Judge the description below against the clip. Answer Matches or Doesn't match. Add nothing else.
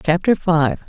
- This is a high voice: Doesn't match